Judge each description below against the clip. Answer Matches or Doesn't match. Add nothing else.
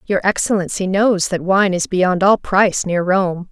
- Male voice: Doesn't match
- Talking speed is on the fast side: Doesn't match